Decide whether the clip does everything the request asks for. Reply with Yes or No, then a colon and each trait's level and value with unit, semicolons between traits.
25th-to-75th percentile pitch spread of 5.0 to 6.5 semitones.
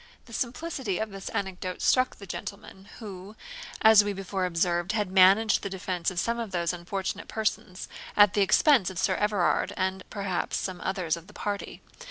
No: narrow, 2.4 semitones